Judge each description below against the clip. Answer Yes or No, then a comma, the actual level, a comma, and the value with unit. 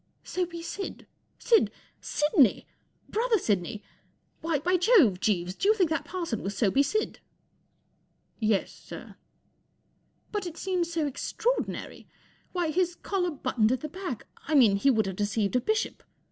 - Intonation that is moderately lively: No, wide, 8.9 semitones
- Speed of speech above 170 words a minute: No, average, 160 wpm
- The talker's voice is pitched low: No, very high, 310 Hz